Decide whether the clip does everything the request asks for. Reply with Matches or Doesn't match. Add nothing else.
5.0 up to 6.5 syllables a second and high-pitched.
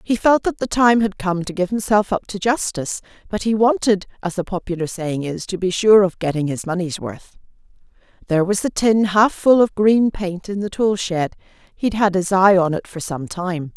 Matches